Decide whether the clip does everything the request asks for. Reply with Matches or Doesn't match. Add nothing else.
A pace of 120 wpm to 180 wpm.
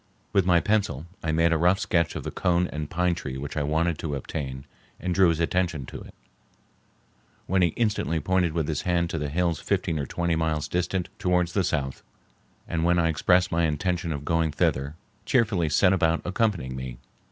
Doesn't match